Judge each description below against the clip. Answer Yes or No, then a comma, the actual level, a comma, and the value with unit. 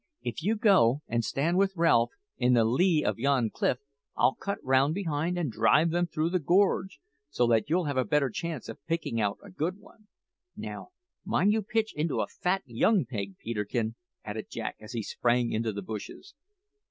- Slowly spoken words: No, average, 190 wpm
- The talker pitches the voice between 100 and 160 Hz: Yes, medium, 140 Hz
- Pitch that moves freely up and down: Yes, wide, 7.4 semitones